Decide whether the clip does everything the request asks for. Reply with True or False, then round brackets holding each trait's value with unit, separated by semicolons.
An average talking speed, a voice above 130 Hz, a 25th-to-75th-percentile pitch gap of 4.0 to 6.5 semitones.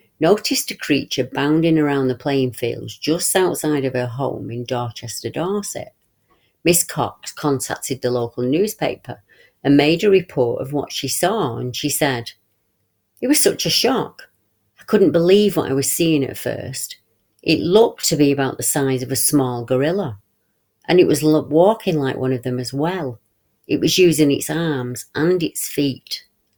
True (170 wpm; 140 Hz; 4.7 semitones)